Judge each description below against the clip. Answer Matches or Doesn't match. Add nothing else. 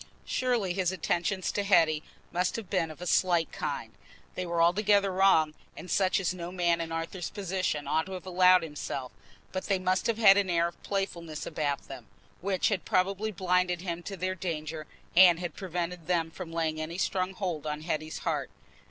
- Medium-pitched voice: Matches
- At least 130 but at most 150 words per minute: Doesn't match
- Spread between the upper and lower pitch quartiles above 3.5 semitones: Doesn't match